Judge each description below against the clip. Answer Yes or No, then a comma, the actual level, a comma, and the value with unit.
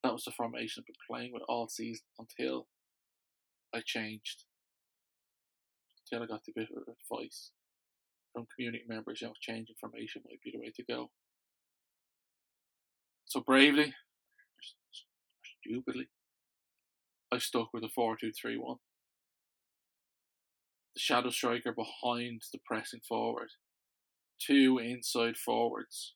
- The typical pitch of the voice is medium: No, low, 115 Hz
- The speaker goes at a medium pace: No, slow, 120 wpm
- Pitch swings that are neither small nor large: No, narrow, 1.9 semitones